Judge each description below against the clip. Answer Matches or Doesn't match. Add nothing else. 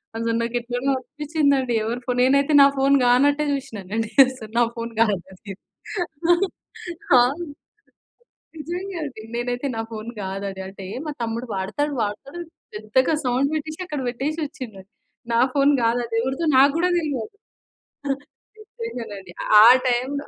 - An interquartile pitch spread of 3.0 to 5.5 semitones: Matches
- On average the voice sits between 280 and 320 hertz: Doesn't match